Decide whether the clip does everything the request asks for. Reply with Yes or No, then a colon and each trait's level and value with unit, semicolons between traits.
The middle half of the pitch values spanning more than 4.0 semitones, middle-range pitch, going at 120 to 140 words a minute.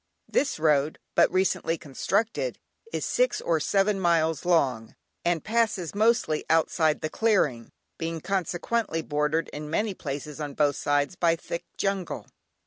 Yes: average, 4.4 semitones; medium, 165 Hz; slow, 135 wpm